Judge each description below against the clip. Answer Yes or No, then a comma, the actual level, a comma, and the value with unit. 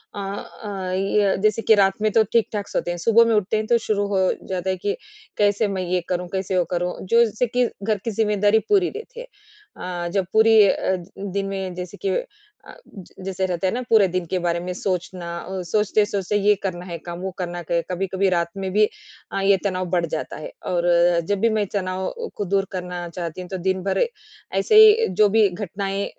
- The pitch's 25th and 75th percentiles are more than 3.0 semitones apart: No, average, 2.7 semitones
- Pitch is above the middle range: Yes, high, 195 Hz